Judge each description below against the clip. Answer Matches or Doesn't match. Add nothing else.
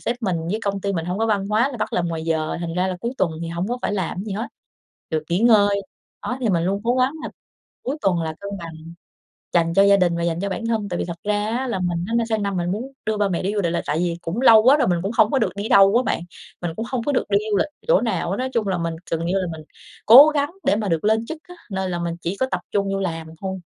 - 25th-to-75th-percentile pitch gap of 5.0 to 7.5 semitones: Doesn't match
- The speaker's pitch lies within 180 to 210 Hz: Matches